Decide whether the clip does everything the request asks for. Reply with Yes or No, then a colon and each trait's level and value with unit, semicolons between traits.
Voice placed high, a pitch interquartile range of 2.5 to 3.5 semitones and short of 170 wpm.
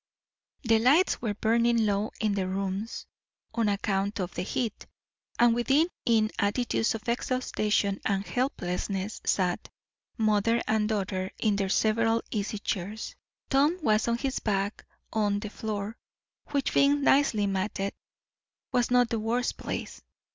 Yes: high, 215 Hz; average, 2.8 semitones; average, 140 wpm